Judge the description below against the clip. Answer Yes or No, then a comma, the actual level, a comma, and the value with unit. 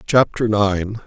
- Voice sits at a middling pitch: No, low, 105 Hz